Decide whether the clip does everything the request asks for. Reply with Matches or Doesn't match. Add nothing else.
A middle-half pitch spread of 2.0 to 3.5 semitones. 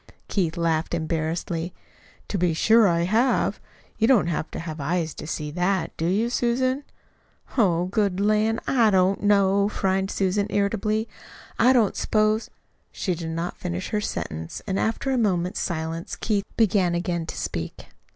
Doesn't match